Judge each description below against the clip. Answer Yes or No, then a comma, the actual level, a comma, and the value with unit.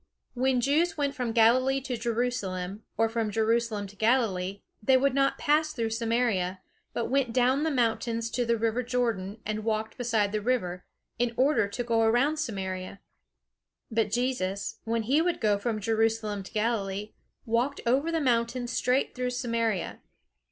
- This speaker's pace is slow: No, average, 160 wpm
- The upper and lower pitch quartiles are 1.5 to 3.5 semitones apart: Yes, average, 2.9 semitones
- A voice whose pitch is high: Yes, high, 230 Hz